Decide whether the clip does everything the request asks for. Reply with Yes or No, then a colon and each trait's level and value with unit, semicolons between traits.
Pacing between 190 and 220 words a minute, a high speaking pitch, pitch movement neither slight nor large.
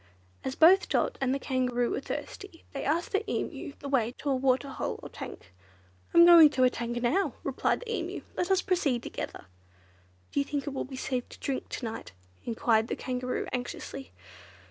Yes: average, 195 wpm; very high, 270 Hz; average, 4.8 semitones